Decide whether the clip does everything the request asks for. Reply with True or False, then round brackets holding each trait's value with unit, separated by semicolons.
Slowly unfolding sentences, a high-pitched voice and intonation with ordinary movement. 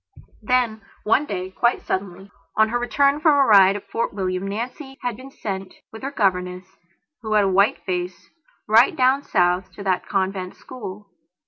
False (175 wpm; 205 Hz; 4.6 semitones)